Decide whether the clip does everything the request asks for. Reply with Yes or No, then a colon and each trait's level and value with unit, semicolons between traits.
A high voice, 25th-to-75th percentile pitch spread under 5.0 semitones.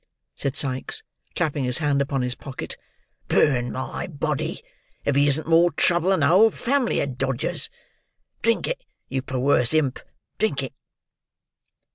No: medium, 140 Hz; average, 3.5 semitones